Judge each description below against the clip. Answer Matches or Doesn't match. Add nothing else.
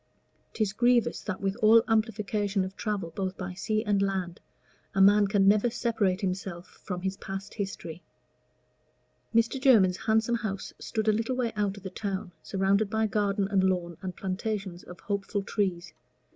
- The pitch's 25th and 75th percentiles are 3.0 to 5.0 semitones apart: Doesn't match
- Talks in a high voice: Matches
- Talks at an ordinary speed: Matches